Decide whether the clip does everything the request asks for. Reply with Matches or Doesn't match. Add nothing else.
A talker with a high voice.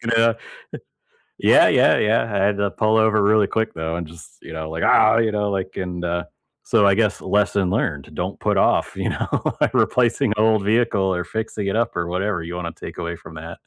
Doesn't match